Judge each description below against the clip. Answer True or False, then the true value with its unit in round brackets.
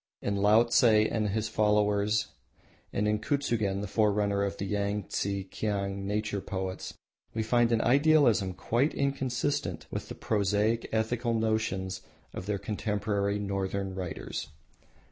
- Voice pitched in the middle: False (105 Hz)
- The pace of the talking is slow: True (125 wpm)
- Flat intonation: True (2.1 semitones)